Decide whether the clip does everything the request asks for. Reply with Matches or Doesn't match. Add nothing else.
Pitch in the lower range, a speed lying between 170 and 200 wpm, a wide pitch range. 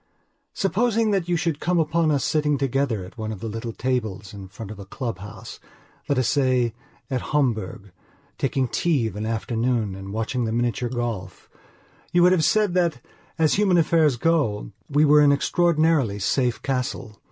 Matches